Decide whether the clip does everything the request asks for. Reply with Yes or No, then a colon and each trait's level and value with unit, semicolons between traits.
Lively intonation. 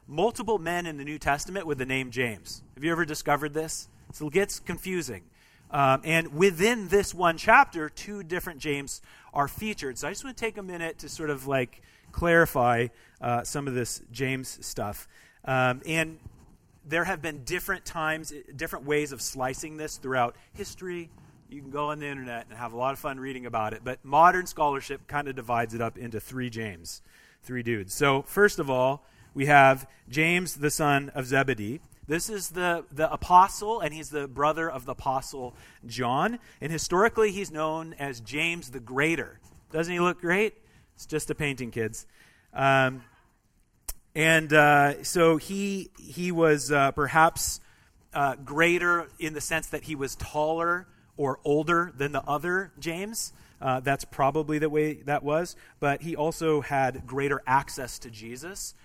No: average, 4.0 semitones